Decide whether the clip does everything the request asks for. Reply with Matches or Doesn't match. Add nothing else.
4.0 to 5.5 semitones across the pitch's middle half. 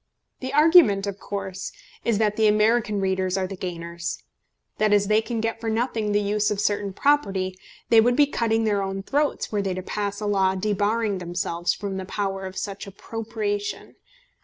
Doesn't match